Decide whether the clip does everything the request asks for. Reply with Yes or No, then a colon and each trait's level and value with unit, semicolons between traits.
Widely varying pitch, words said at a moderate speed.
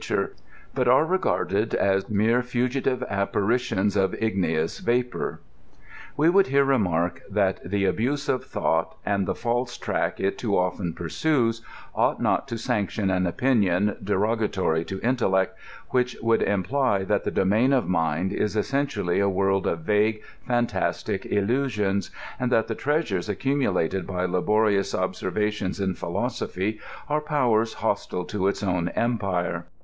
No: average, 4.5 semitones; average, 145 wpm